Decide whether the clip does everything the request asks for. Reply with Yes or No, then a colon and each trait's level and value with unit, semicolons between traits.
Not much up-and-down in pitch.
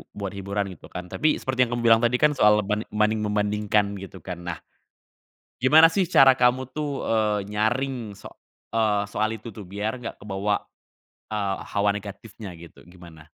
No: average, 3.1 semitones